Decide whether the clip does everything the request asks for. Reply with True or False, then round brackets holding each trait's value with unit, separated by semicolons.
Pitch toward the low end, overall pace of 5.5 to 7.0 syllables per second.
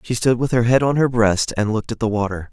True (115 Hz; 6.2 syllables/s)